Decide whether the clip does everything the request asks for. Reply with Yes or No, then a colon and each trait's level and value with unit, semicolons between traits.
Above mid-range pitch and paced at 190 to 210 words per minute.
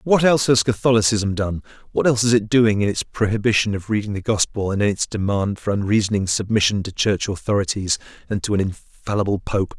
No: low, 105 Hz; average, 195 wpm